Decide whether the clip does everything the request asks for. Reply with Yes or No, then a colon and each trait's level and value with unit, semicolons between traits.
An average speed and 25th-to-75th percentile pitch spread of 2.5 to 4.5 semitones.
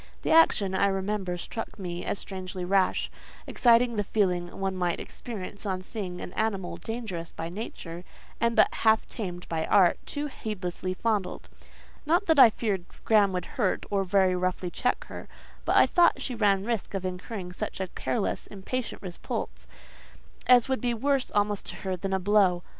Yes: average, 175 wpm; average, 3.7 semitones